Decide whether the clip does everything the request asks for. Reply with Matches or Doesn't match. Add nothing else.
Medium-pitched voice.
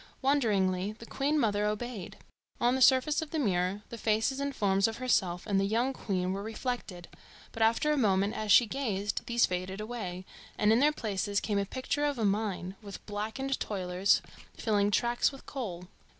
Doesn't match